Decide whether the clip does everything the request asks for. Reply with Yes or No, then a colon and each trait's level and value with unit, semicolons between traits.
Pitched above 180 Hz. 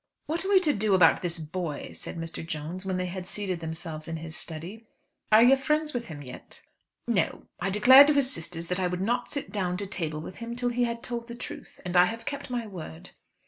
Yes: high, 190 Hz